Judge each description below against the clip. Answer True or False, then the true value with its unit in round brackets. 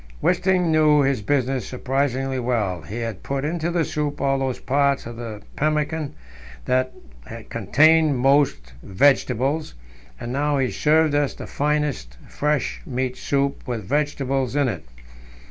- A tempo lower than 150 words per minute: True (140 wpm)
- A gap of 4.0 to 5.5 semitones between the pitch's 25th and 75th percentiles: False (2.9 semitones)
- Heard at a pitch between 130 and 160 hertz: True (140 Hz)